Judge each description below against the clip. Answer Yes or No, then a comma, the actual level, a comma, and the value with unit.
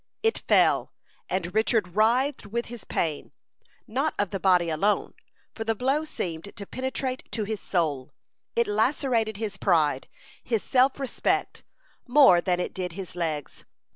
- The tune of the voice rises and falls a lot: Yes, wide, 5.8 semitones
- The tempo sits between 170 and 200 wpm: No, average, 150 wpm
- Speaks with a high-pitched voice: Yes, high, 210 Hz